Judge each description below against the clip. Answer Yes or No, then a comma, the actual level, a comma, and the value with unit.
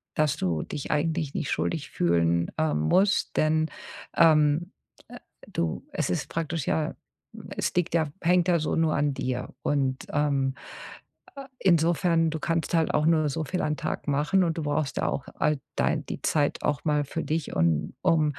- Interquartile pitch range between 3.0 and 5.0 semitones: No, narrow, 2.6 semitones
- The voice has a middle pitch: Yes, medium, 155 Hz